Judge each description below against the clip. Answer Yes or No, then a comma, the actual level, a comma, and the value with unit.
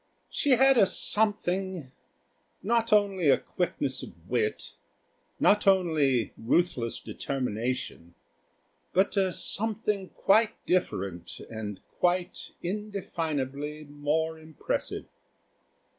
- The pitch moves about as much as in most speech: No, wide, 6.5 semitones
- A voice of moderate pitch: Yes, medium, 175 Hz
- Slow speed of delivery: Yes, slow, 85 wpm